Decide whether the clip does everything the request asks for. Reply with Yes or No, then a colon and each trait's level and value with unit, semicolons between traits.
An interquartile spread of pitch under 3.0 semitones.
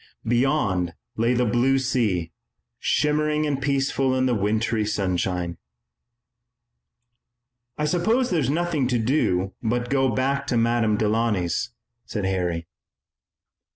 No: average, 4.9 semitones